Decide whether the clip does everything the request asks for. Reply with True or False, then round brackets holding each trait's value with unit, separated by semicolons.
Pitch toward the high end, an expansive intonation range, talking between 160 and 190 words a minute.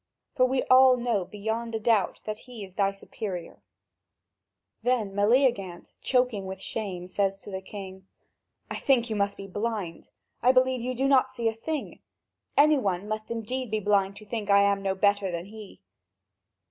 False (210 Hz; 3.7 semitones; 175 wpm)